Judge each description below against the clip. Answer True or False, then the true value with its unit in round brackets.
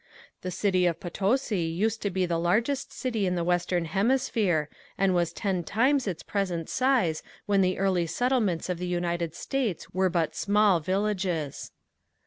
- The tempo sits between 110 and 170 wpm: True (160 wpm)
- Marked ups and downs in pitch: False (3.5 semitones)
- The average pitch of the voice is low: False (185 Hz)